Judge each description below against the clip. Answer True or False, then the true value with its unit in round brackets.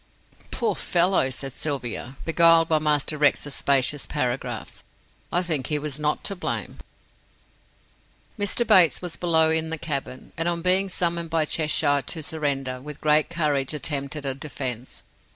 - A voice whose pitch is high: False (150 Hz)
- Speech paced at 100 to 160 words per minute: True (150 wpm)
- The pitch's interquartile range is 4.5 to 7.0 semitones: False (3.2 semitones)